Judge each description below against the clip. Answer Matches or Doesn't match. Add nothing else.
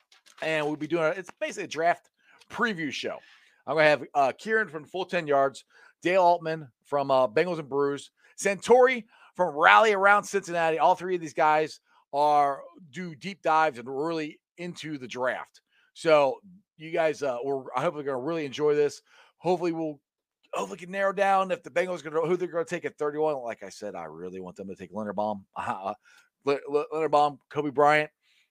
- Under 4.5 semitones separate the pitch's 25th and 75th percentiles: Matches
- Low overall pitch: Doesn't match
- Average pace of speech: Matches